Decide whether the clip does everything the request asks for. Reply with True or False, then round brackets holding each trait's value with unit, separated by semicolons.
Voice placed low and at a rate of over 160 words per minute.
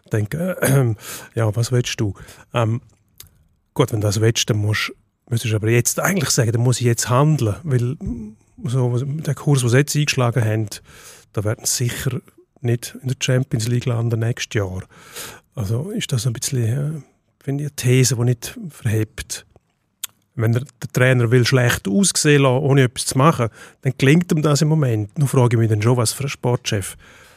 True (125 Hz; 185 wpm)